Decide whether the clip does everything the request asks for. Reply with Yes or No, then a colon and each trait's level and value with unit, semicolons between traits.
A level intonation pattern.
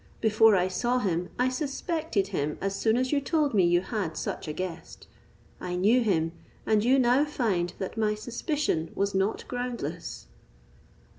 No: wide, 5.4 semitones